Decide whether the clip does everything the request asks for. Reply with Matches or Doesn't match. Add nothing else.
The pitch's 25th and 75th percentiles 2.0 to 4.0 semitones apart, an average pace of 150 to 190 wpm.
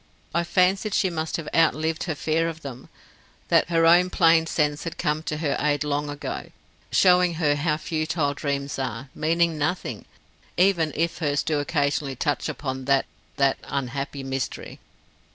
Matches